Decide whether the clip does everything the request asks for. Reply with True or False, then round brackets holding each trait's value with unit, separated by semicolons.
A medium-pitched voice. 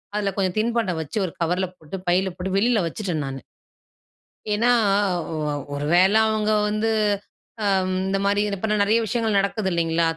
False (195 Hz)